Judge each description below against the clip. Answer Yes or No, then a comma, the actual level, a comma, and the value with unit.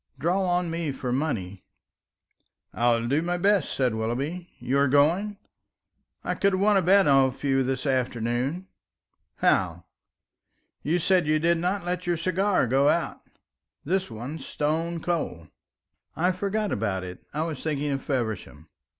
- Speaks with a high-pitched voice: No, medium, 150 Hz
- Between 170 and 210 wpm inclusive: No, average, 160 wpm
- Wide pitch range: Yes, wide, 5.8 semitones